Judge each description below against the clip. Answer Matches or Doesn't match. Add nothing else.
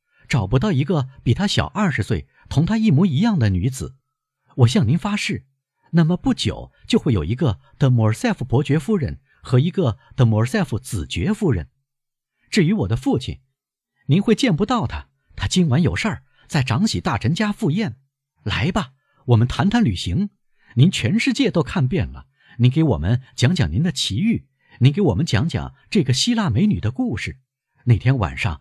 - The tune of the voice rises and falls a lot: Matches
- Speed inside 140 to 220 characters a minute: Doesn't match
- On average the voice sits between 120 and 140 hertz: Matches